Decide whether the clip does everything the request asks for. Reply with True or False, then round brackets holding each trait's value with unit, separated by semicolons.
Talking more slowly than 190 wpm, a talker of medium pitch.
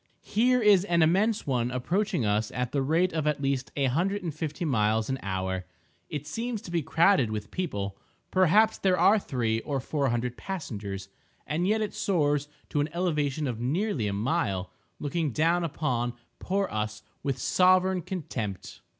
True (165 wpm; 145 Hz)